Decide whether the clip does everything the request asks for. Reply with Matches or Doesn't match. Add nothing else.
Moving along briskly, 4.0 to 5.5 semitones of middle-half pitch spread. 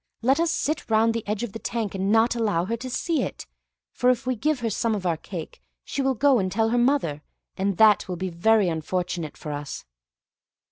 Matches